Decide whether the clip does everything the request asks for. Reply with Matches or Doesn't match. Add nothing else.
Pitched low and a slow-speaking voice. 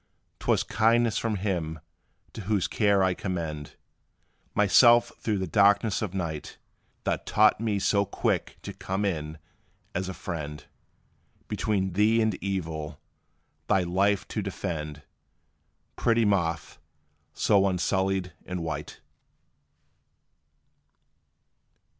Matches